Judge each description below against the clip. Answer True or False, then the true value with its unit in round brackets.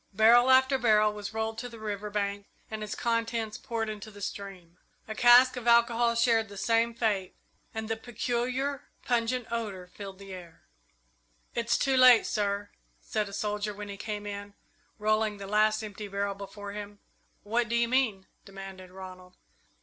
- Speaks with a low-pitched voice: False (215 Hz)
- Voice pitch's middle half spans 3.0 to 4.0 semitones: False (2.6 semitones)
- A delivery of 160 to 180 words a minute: True (170 wpm)